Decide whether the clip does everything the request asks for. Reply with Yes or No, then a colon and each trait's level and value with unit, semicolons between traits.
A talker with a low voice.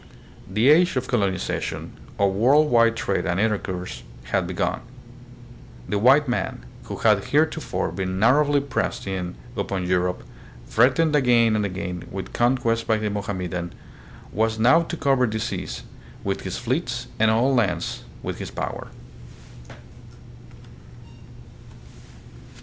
Yes: low, 110 Hz